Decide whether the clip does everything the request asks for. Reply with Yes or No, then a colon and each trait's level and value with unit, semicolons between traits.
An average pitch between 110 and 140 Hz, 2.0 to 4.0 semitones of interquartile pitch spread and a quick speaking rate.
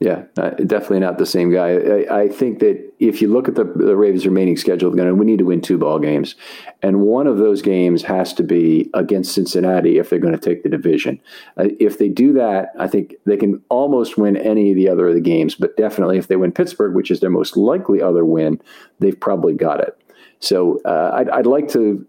No: very low, 95 Hz; average, 2.9 semitones; fast, 235 wpm